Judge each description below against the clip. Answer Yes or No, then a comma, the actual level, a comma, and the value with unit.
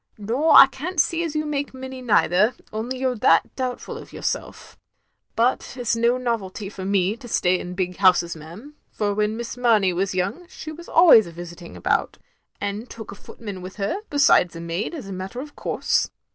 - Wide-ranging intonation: Yes, wide, 5.7 semitones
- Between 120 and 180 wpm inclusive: No, average, 200 wpm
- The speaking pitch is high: Yes, high, 220 Hz